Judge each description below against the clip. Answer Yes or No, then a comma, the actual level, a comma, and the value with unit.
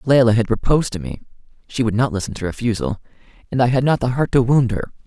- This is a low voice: Yes, low, 115 Hz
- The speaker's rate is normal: No, fast, 235 wpm